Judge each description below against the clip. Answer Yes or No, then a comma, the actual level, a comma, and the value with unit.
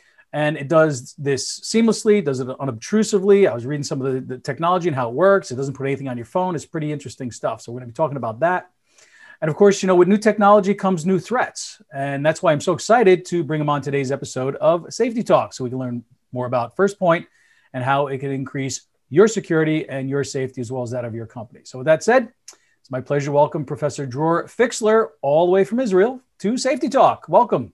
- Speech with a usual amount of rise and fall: No, wide, 6.4 semitones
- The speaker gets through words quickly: Yes, fast, 240 wpm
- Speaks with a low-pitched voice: No, medium, 150 Hz